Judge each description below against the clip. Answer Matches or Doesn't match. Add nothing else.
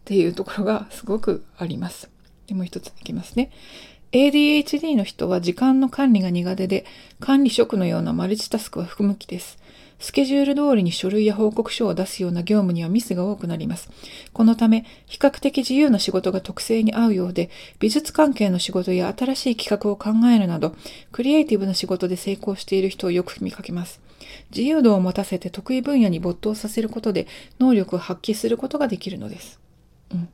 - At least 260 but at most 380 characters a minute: Doesn't match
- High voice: Matches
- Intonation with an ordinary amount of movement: Matches